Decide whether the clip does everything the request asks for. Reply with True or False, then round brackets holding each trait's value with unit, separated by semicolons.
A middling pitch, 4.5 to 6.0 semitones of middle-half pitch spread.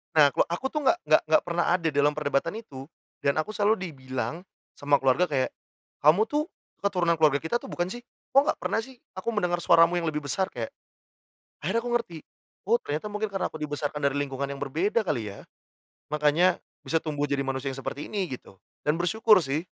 True (155 Hz; 5.0 semitones)